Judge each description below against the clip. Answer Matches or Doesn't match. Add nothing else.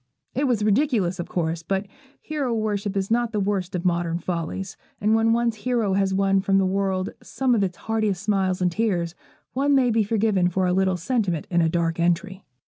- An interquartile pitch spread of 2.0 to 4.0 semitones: Matches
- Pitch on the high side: Matches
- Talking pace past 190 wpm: Matches